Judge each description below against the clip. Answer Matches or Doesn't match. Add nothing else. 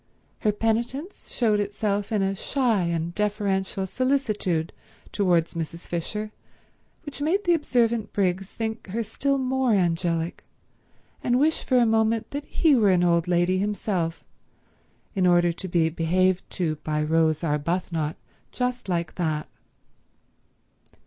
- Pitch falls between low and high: Doesn't match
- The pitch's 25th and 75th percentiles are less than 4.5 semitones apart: Doesn't match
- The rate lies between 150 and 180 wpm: Doesn't match